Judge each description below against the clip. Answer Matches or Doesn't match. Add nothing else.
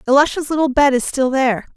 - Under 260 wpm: Matches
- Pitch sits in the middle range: Doesn't match